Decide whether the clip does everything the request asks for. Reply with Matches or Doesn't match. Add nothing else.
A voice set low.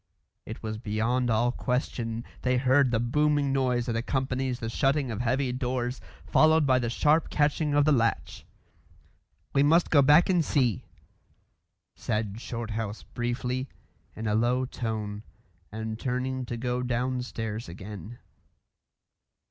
Matches